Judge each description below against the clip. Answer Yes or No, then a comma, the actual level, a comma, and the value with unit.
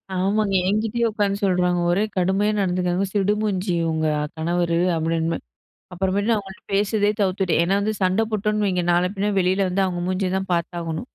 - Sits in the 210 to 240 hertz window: No, high, 190 Hz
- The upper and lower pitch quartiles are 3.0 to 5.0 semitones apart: No, narrow, 2.5 semitones